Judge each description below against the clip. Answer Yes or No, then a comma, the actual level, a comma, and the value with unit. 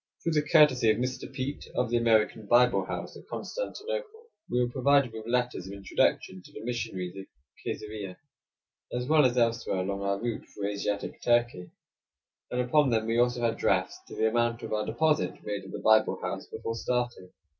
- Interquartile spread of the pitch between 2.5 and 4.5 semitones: Yes, average, 3.0 semitones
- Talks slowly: No, average, 190 wpm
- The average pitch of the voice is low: Yes, low, 120 Hz